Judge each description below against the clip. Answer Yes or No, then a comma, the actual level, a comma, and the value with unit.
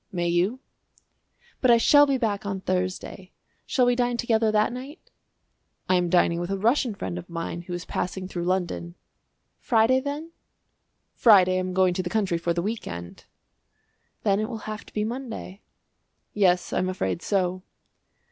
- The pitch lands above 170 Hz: Yes, high, 190 Hz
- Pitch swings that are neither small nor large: Yes, average, 4.4 semitones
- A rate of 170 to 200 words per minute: Yes, average, 175 wpm